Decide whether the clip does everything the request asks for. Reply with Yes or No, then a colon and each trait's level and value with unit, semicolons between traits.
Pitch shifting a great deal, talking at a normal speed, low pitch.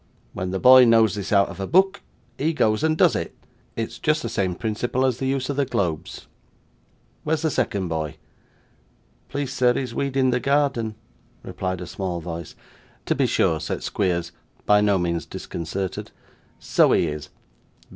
Yes: wide, 6.6 semitones; average, 165 wpm; low, 110 Hz